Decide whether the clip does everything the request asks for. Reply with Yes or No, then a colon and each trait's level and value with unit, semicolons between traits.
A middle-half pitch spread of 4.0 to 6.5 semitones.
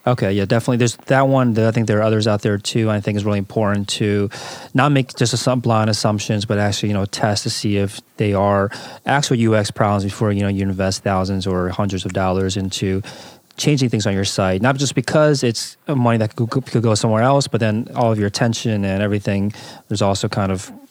No: average, 3.4 semitones